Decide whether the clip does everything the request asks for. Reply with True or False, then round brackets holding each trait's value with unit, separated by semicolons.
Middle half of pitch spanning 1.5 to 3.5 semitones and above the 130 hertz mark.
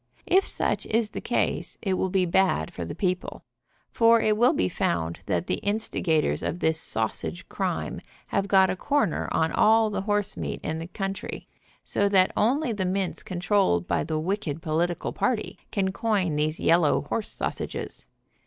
False (4.6 semitones; 190 Hz)